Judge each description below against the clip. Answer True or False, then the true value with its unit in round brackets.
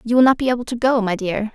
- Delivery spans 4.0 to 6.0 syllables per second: False (6.9 syllables/s)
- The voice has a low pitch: False (235 Hz)